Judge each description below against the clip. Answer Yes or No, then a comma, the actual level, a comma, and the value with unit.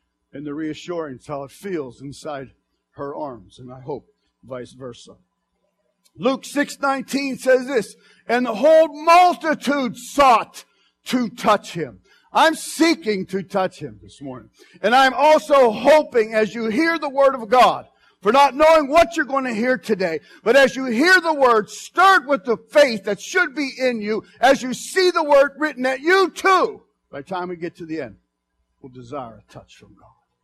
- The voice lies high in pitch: Yes, high, 245 Hz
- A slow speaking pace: No, average, 180 wpm